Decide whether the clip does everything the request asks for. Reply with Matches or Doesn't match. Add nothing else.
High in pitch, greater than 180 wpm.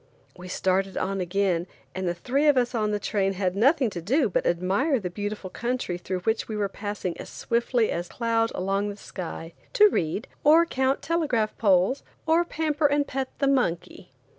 Matches